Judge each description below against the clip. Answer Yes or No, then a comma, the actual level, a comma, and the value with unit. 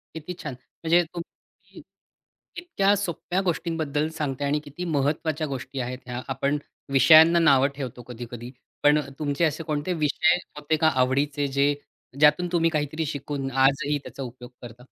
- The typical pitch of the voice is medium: Yes, medium, 145 Hz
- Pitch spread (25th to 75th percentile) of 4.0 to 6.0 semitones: No, average, 3.1 semitones